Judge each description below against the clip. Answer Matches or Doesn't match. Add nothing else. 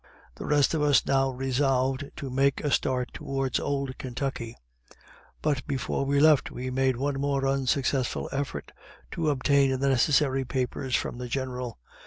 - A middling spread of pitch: Doesn't match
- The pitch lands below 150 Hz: Matches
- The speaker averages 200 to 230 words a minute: Doesn't match